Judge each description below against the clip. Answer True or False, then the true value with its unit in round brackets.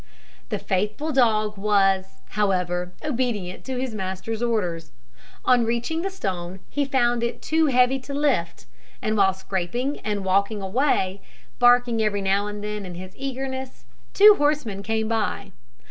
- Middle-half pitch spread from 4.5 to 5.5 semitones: True (4.8 semitones)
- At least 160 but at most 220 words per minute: False (145 wpm)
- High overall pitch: True (215 Hz)